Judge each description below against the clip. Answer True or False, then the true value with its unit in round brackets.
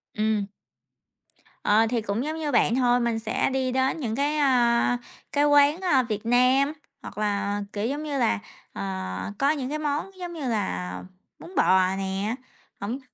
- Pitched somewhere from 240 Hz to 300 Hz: True (245 Hz)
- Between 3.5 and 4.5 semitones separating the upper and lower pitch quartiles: False (5.2 semitones)